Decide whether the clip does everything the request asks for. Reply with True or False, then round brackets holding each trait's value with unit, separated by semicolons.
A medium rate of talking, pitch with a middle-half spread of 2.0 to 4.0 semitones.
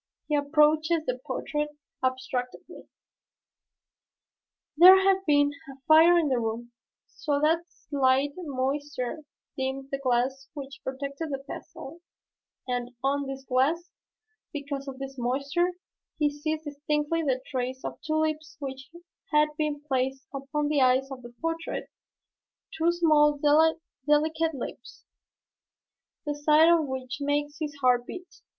False (130 wpm; 2.8 semitones)